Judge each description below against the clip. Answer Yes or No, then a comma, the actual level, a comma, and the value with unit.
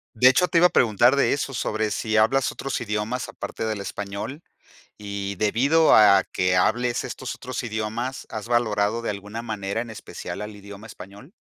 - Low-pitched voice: Yes, low, 110 Hz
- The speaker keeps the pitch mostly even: No, average, 3.3 semitones